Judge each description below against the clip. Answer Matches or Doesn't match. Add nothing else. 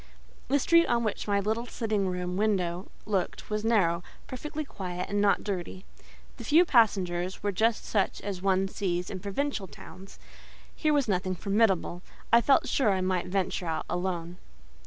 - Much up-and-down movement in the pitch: Doesn't match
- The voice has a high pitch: Matches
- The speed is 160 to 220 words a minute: Matches